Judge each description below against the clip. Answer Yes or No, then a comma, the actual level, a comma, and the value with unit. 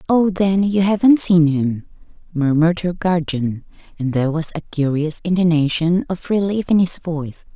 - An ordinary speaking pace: Yes, average, 160 wpm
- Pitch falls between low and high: Yes, medium, 170 Hz